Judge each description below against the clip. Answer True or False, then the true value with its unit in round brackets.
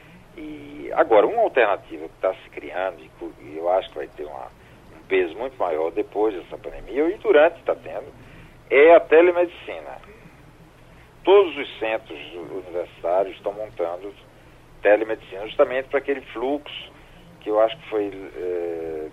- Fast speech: False (145 wpm)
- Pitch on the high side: False (140 Hz)